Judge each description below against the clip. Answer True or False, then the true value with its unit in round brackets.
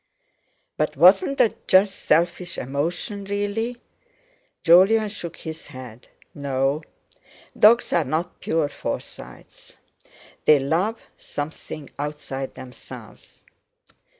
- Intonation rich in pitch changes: True (5.9 semitones)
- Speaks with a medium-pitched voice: True (165 Hz)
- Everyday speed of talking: False (95 wpm)